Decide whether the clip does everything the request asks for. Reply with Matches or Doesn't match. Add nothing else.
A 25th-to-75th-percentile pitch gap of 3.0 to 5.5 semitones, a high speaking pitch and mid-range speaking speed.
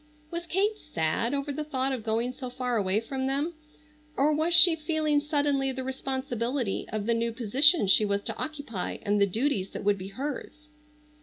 Matches